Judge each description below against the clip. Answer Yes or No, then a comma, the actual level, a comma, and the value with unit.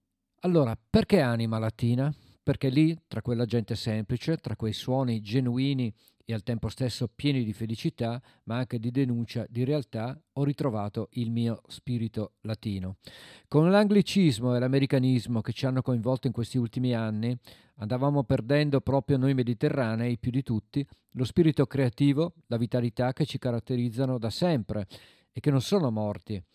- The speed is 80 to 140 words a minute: No, average, 155 wpm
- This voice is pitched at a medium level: No, low, 125 Hz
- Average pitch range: Yes, average, 3.3 semitones